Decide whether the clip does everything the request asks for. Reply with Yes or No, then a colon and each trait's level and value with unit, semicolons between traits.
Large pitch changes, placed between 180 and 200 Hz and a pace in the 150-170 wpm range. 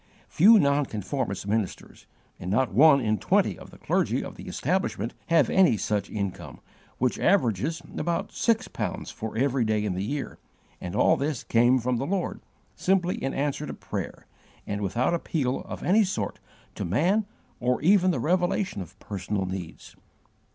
No: wide, 8.4 semitones; low, 130 Hz; average, 165 wpm